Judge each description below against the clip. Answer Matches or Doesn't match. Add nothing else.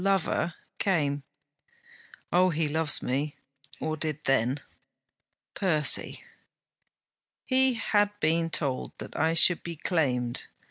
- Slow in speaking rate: Matches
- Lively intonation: Doesn't match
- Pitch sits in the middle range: Matches